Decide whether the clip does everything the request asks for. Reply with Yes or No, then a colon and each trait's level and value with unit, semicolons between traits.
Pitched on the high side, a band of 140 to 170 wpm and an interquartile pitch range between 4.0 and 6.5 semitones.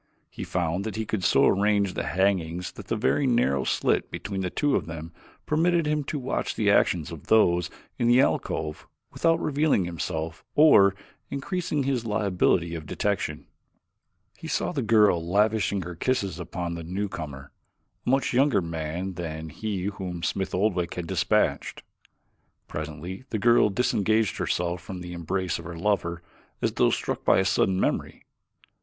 No: very low, 95 Hz; average, 160 wpm; average, 4.6 semitones